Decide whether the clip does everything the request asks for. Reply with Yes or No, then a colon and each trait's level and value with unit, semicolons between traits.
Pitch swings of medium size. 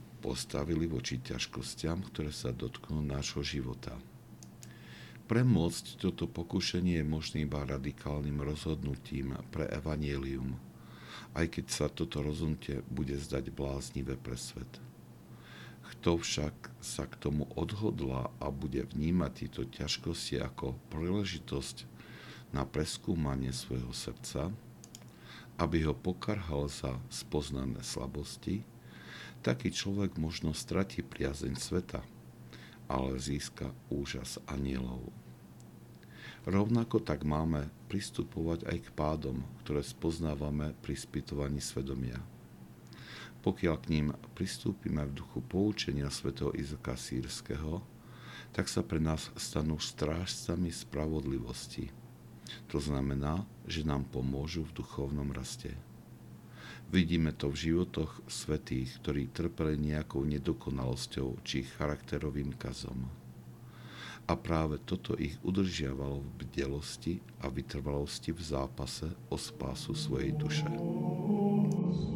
Yes: average, 3.8 semitones